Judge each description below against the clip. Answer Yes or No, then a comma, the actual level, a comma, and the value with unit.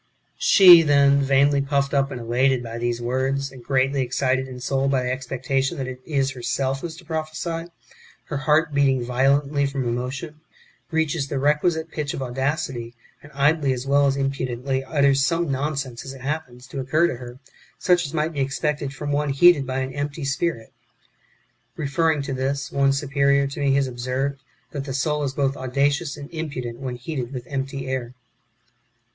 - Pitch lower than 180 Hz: Yes, medium, 140 Hz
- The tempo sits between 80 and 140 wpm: No, average, 185 wpm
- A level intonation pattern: Yes, narrow, 1.9 semitones